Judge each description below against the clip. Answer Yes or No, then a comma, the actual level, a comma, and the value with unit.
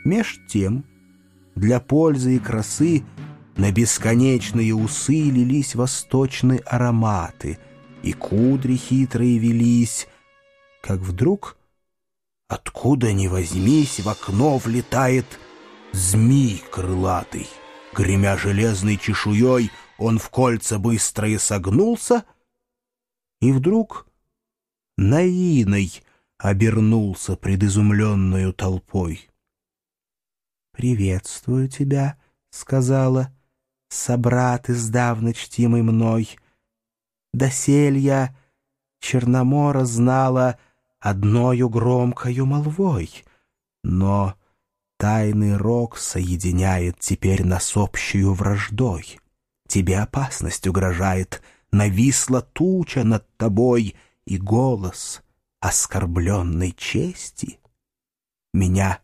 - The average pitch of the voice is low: Yes, low, 115 Hz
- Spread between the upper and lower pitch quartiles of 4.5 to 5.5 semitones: Yes, average, 4.8 semitones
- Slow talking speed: Yes, slow, 75 wpm